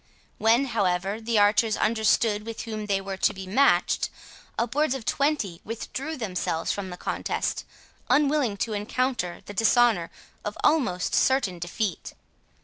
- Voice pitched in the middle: No, high, 220 Hz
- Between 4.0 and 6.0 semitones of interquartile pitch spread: Yes, average, 4.3 semitones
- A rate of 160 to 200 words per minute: No, average, 140 wpm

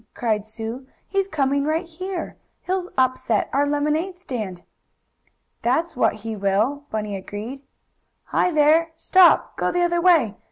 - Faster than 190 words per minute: No, slow, 135 wpm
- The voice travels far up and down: Yes, wide, 7.4 semitones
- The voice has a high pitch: Yes, very high, 285 Hz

